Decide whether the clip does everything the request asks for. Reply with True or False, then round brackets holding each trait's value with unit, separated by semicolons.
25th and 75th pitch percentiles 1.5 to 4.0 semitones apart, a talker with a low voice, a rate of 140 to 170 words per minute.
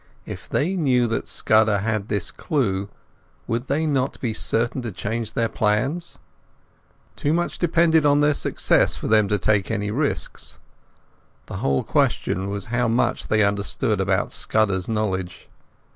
False (5.3 semitones; 110 Hz; 150 wpm)